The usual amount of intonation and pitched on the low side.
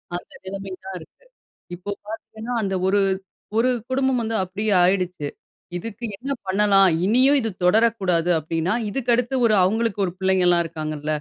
No: average, 4.1 semitones; high, 195 Hz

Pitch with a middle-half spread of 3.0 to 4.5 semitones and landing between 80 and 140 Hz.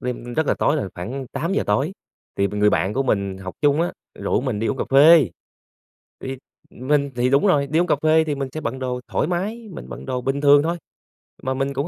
Yes: average, 4.1 semitones; low, 135 Hz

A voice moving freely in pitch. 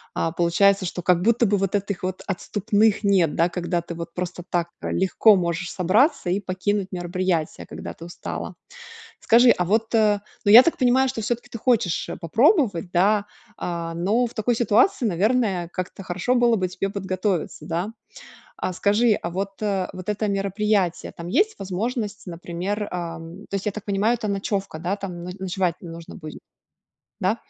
No: average, 3.4 semitones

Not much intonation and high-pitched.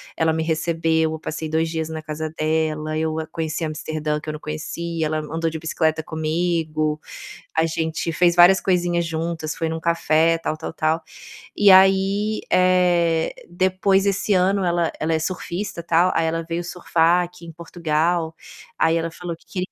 No: narrow, 1.7 semitones; medium, 165 Hz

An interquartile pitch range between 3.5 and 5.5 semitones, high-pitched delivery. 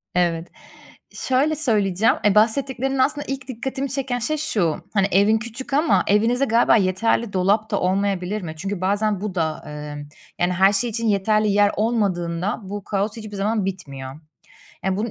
Yes: average, 4.0 semitones; high, 205 Hz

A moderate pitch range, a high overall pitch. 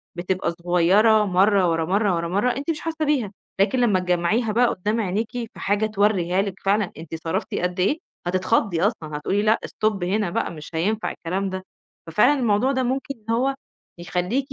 Yes: average, 4.2 semitones; high, 200 Hz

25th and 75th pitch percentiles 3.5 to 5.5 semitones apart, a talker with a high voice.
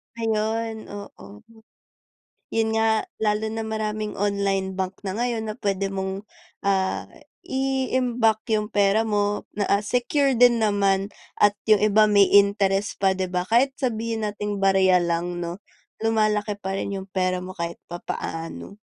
No: narrow, 2.4 semitones; high, 205 Hz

